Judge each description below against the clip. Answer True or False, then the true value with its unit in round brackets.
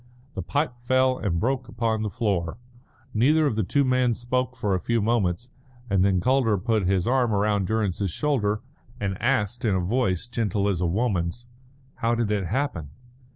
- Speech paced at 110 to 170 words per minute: False (180 wpm)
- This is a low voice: True (110 Hz)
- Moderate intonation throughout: True (4.2 semitones)